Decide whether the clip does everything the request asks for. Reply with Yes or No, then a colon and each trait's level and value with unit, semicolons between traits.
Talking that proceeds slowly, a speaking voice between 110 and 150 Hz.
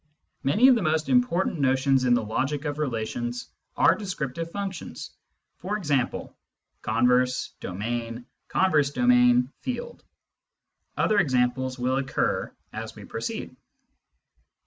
Yes: slow, 120 wpm; low, 135 Hz